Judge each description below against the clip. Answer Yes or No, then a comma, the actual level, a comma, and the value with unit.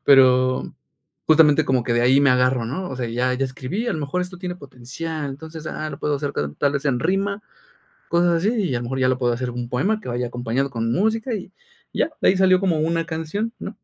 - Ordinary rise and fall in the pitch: No, wide, 5.9 semitones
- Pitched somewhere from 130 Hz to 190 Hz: Yes, medium, 140 Hz